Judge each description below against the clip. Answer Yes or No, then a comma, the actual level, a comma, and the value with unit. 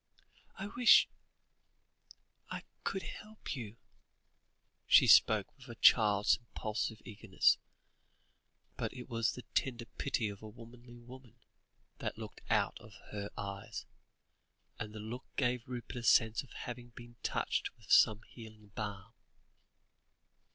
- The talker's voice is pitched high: No, low, 115 Hz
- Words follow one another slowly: Yes, slow, 130 wpm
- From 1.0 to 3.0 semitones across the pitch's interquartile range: Yes, narrow, 2.5 semitones